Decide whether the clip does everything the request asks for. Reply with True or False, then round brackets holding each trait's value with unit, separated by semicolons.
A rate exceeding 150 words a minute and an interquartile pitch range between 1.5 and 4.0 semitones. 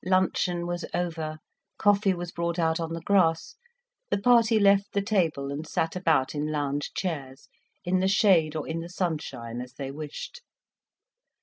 True (165 wpm; 3.5 semitones)